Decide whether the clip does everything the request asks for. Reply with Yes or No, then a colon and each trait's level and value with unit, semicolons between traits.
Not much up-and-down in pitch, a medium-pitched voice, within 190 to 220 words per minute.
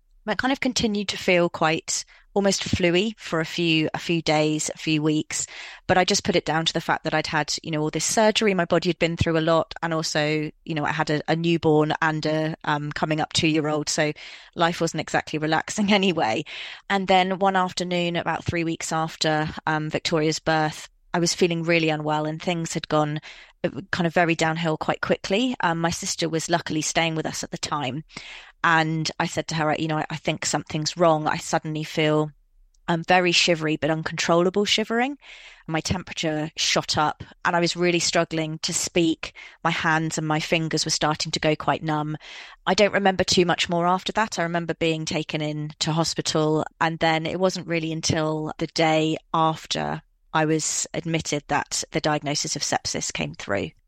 Yes: narrow, 1.9 semitones; medium, 160 Hz; average, 200 wpm